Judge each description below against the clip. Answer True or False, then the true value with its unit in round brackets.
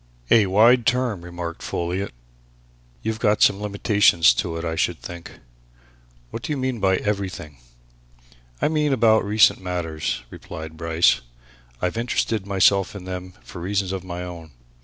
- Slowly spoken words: False (150 wpm)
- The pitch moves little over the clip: False (3.8 semitones)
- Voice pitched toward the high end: False (95 Hz)